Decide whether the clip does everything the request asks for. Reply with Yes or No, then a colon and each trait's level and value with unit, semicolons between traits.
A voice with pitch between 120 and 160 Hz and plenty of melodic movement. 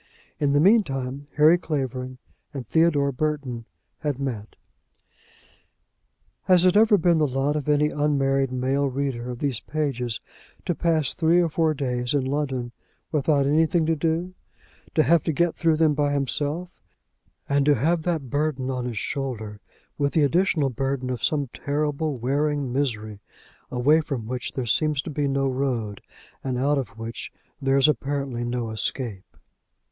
No: medium, 140 Hz; average, 3.2 semitones